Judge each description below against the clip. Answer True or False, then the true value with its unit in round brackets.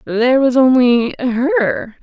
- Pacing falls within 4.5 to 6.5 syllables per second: False (3.4 syllables/s)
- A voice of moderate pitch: False (245 Hz)